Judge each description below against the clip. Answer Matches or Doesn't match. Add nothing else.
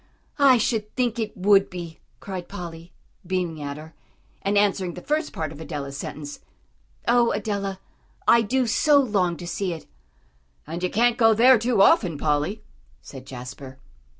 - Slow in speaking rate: Doesn't match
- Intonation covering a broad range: Matches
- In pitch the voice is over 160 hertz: Matches